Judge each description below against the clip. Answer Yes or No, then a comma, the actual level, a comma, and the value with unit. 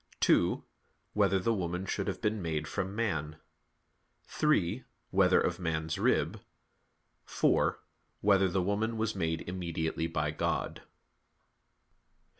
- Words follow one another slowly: Yes, slow, 115 wpm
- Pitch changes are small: No, average, 4.0 semitones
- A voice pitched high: No, very low, 95 Hz